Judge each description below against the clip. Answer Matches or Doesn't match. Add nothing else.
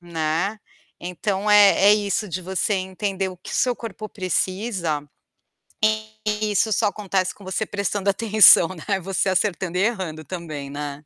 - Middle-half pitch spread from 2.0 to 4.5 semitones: Matches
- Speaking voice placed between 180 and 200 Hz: Matches